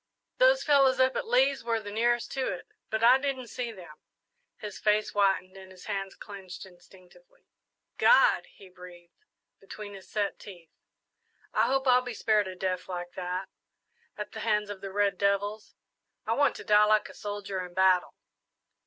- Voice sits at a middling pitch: No, high, 205 Hz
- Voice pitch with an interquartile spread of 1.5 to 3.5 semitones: No, average, 4.1 semitones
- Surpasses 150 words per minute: Yes, average, 175 wpm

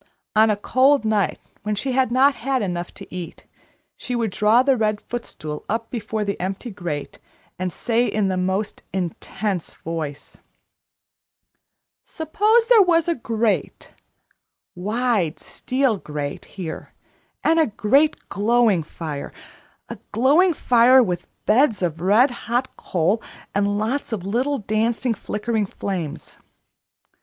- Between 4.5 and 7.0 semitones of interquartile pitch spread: Yes, average, 5.1 semitones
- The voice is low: No, high, 220 Hz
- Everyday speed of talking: No, slow, 130 wpm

